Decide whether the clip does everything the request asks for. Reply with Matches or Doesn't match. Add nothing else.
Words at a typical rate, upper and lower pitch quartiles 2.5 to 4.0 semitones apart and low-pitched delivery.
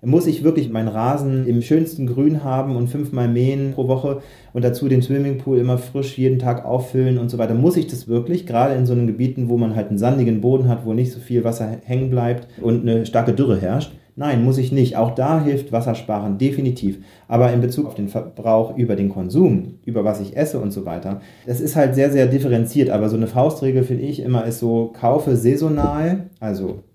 Doesn't match